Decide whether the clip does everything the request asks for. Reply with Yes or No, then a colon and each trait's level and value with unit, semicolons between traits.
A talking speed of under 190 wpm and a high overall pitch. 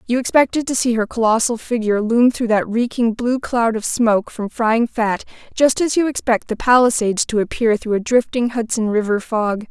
No: average, 200 wpm; high, 230 Hz